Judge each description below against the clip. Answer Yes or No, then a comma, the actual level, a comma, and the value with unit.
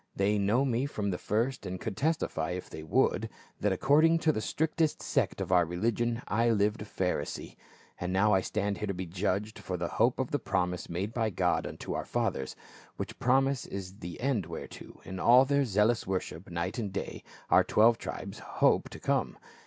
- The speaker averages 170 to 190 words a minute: No, average, 200 wpm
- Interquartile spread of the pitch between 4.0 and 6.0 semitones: Yes, average, 4.5 semitones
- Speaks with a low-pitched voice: Yes, low, 105 Hz